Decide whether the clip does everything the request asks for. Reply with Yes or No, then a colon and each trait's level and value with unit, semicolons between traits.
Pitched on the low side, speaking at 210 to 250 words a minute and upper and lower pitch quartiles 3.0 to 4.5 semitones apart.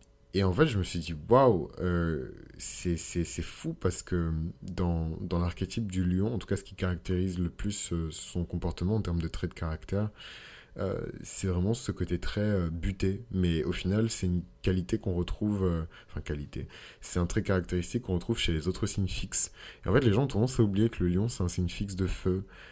No: very low, 90 Hz; fast, 220 wpm; narrow, 2.5 semitones